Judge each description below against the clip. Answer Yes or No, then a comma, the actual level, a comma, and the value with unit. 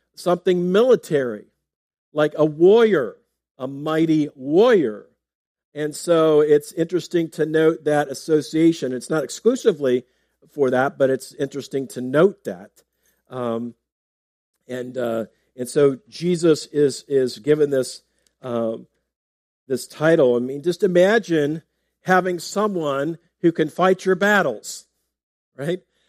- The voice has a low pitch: No, medium, 150 Hz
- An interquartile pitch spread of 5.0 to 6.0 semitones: Yes, wide, 5.6 semitones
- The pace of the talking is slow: Yes, slow, 120 wpm